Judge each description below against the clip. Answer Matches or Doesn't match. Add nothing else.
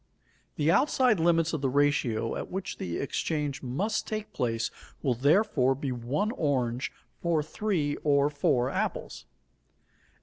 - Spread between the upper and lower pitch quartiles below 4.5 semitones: Doesn't match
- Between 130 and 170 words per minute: Matches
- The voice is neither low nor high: Matches